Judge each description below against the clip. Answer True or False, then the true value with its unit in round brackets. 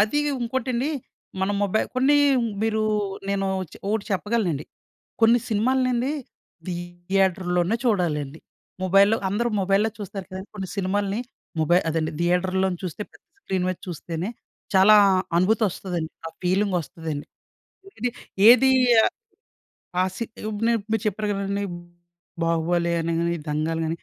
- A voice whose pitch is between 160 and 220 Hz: True (190 Hz)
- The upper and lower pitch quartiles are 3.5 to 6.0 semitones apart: True (3.8 semitones)